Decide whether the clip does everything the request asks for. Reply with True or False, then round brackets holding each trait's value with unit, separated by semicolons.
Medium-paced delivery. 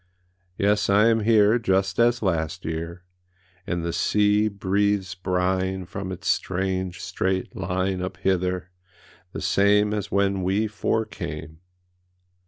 False (130 wpm)